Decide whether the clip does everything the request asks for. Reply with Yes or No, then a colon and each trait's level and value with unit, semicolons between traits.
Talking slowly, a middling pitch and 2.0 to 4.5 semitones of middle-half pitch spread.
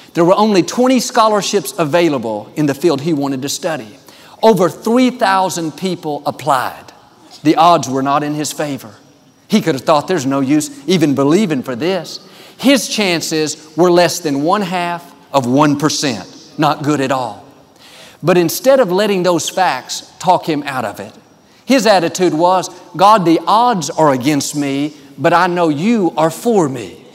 No: average, 165 wpm; medium, 165 Hz; average, 4.2 semitones